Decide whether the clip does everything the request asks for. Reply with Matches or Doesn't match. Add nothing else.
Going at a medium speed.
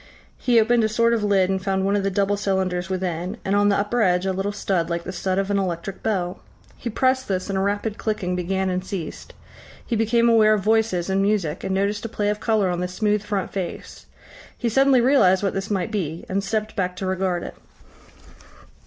Doesn't match